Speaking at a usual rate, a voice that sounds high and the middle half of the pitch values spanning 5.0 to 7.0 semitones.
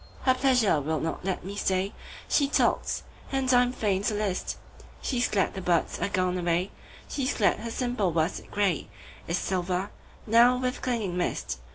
Yes: average, 155 wpm; high, 200 Hz; wide, 5.5 semitones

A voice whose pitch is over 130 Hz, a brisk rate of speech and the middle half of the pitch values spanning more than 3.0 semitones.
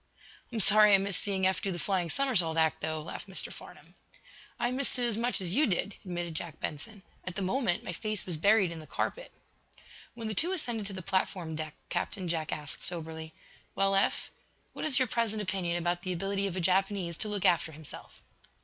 Yes: high, 190 Hz; fast, 210 wpm; average, 3.9 semitones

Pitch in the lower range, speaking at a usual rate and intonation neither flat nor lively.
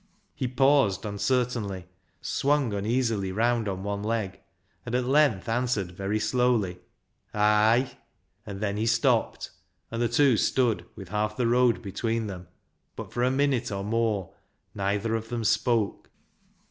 Yes: low, 115 Hz; average, 150 wpm; average, 3.3 semitones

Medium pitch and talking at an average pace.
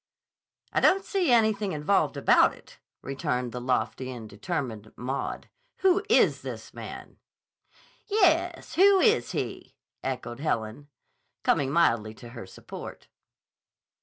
No: medium, 145 Hz; slow, 120 wpm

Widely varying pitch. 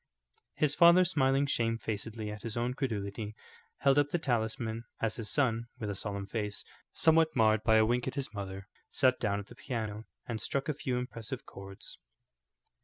No: average, 3.9 semitones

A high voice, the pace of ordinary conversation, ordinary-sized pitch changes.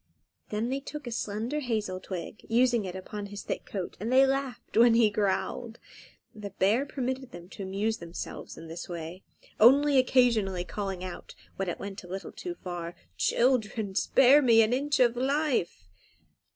Yes: high, 220 Hz; average, 170 wpm; average, 5.0 semitones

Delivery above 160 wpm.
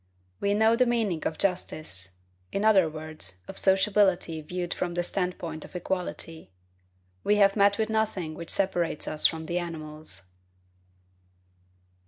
No: average, 140 wpm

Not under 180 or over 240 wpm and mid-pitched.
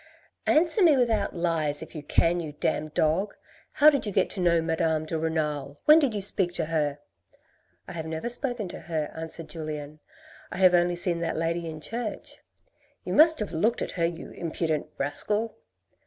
Yes: average, 200 wpm; medium, 170 Hz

